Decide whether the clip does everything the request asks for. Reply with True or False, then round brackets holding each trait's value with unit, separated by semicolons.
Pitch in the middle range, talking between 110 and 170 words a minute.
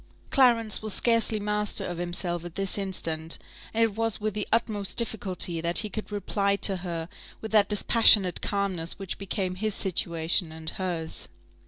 False (195 Hz; 165 wpm)